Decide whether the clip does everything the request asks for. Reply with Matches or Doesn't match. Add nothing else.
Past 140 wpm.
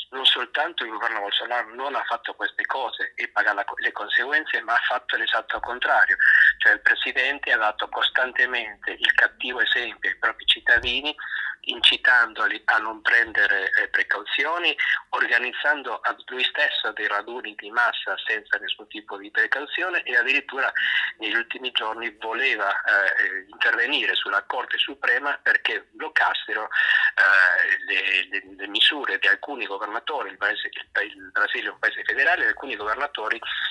Matches